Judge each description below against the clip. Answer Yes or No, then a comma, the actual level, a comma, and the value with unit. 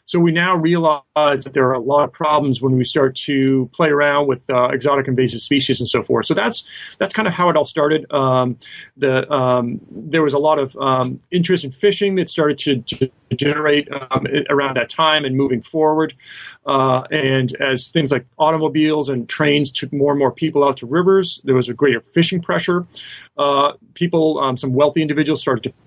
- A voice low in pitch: No, medium, 145 Hz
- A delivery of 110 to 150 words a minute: No, fast, 205 wpm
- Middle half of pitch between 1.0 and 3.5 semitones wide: Yes, average, 2.9 semitones